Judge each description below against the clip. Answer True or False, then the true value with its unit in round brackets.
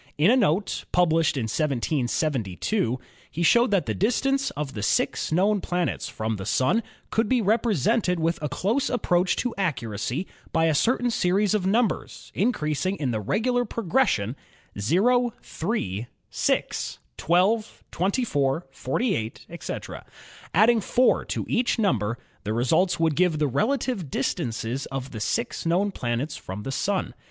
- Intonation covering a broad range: True (8.5 semitones)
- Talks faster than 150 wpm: False (145 wpm)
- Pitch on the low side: False (175 Hz)